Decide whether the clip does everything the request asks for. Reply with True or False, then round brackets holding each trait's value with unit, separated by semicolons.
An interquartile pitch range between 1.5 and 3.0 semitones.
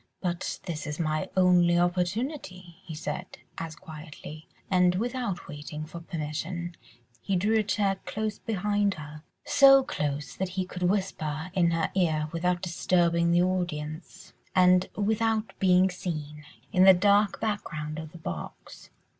False (3.4 semitones)